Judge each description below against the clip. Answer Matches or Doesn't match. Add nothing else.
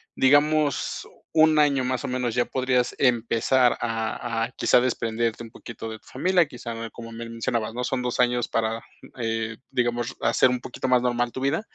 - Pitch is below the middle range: Matches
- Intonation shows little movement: Matches